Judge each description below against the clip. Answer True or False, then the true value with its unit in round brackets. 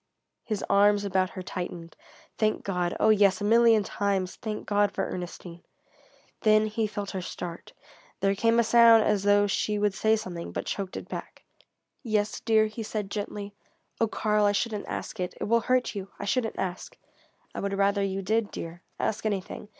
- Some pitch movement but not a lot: False (2.0 semitones)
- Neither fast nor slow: True (185 wpm)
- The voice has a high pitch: True (205 Hz)